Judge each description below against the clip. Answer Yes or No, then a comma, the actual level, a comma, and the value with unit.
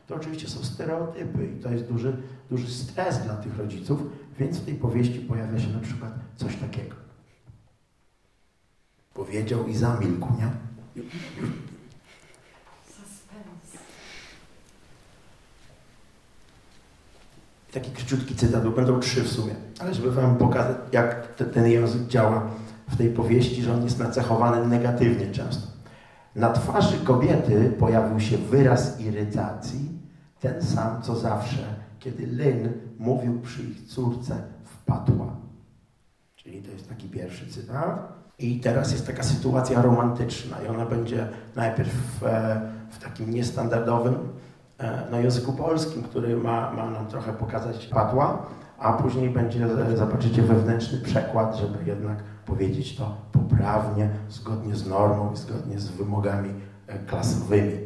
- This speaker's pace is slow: No, average, 125 wpm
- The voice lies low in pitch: Yes, low, 120 Hz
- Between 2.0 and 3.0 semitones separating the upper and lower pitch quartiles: Yes, average, 2.7 semitones